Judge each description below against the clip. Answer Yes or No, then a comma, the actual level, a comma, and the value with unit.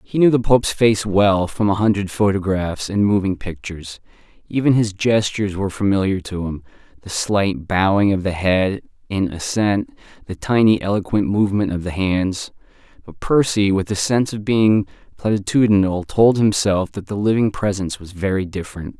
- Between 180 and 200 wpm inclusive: No, average, 165 wpm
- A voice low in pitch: Yes, low, 100 Hz